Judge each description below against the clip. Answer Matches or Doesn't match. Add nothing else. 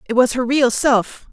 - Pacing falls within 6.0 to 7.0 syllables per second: Doesn't match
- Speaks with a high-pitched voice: Matches